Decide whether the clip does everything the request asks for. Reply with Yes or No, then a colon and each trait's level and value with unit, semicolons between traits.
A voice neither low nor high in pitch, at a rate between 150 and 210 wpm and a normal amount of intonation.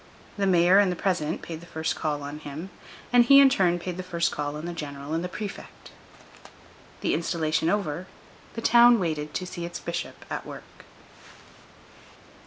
Yes: medium, 170 Hz; average, 180 wpm; average, 3.4 semitones